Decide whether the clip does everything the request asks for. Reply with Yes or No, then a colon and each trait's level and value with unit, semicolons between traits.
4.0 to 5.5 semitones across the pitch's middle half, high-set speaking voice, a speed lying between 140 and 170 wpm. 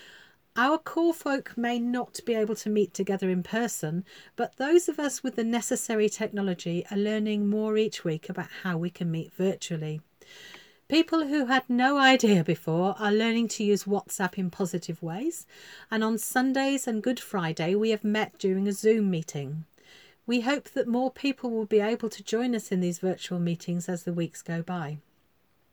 No: average, 5.1 semitones; high, 215 Hz; average, 180 wpm